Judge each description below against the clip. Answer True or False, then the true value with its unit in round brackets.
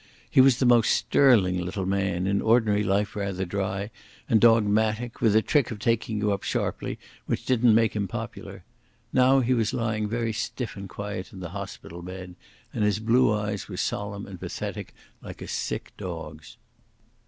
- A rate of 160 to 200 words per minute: True (175 wpm)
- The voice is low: True (105 Hz)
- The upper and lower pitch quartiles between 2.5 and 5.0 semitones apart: True (2.8 semitones)